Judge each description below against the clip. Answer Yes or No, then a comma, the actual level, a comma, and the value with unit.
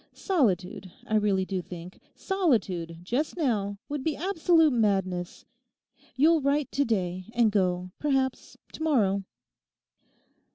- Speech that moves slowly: Yes, slow, 120 wpm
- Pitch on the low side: No, high, 215 Hz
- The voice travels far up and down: Yes, wide, 7.9 semitones